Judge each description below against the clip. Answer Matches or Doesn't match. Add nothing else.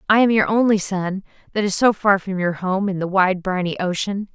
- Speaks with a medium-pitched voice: Doesn't match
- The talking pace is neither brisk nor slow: Doesn't match